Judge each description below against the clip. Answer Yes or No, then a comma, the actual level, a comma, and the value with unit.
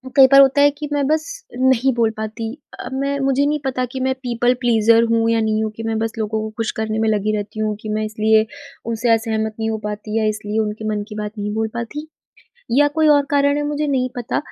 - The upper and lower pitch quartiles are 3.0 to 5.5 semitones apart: Yes, average, 3.7 semitones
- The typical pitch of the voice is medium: No, high, 225 Hz